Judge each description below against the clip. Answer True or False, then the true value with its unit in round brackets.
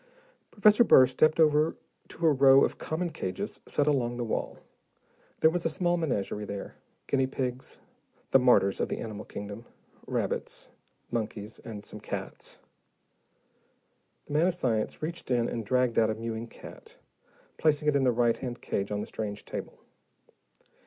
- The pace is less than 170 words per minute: True (160 wpm)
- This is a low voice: True (125 Hz)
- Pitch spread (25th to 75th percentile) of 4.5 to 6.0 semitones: True (5.5 semitones)